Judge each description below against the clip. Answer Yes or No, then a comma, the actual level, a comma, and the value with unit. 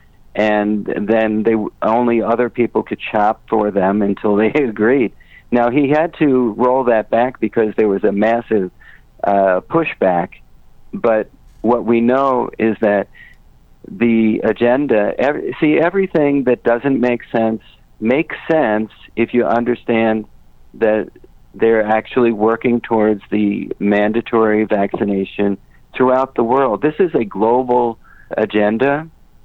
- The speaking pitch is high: No, low, 115 Hz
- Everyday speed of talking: No, slow, 130 wpm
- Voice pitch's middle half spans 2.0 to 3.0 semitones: Yes, narrow, 2.5 semitones